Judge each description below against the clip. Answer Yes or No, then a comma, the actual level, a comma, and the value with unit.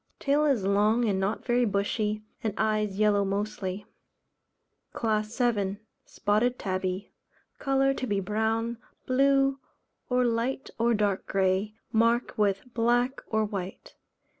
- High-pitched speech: Yes, high, 215 Hz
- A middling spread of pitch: Yes, average, 3.2 semitones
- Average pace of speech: No, slow, 125 wpm